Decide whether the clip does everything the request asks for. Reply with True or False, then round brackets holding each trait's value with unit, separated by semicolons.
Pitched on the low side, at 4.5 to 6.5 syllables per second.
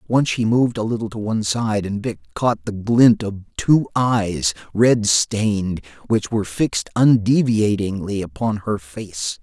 False (105 Hz; 4.3 syllables/s)